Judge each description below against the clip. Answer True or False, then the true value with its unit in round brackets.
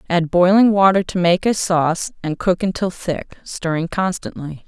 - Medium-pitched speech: True (180 Hz)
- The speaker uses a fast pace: False (165 wpm)